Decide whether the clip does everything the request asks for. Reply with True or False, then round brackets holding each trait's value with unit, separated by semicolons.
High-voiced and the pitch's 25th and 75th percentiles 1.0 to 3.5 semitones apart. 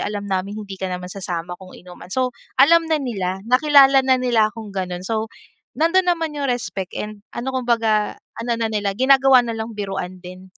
False (220 Hz; 5.1 semitones)